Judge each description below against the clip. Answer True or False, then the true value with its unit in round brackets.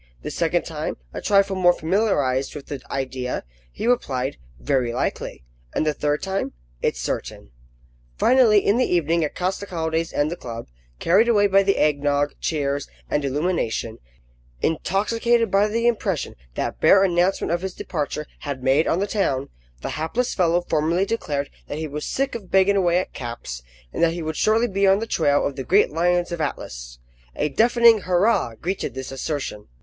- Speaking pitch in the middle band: True (170 Hz)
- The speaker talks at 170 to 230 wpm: True (180 wpm)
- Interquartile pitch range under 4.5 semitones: False (5.6 semitones)